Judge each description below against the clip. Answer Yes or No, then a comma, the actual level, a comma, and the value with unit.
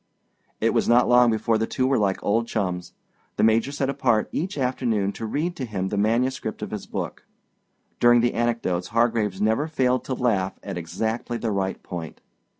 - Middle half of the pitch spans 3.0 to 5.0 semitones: Yes, average, 3.5 semitones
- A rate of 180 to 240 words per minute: Yes, average, 185 wpm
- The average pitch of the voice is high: No, low, 115 Hz